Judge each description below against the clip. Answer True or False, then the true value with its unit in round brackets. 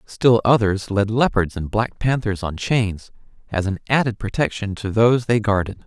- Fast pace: False (175 wpm)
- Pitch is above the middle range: False (105 Hz)